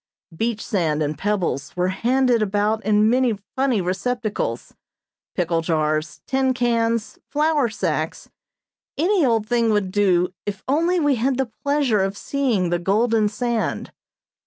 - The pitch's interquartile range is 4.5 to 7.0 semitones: Yes, average, 5.1 semitones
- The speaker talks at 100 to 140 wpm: Yes, slow, 135 wpm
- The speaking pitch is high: Yes, high, 220 Hz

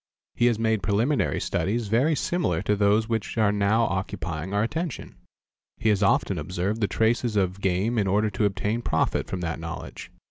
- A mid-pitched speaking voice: No, low, 105 Hz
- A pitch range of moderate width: Yes, average, 3.0 semitones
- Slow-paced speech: No, average, 180 wpm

